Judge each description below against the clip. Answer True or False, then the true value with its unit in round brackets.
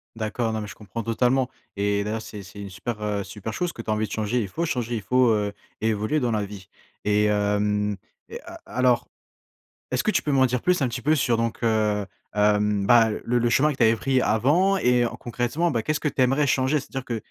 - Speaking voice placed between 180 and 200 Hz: False (115 Hz)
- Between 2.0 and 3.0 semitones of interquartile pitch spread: False (3.5 semitones)